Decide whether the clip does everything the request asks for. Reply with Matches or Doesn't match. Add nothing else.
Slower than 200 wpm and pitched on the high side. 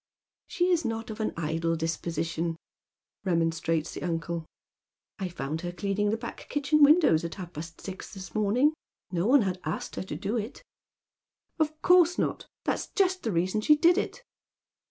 Matches